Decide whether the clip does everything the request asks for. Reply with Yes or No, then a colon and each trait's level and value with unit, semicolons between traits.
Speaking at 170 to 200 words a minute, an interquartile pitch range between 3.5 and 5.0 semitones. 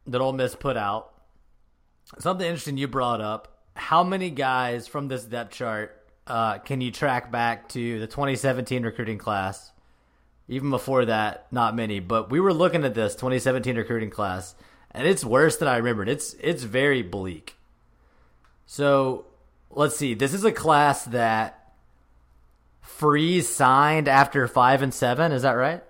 No: average, 160 wpm; average, 4.4 semitones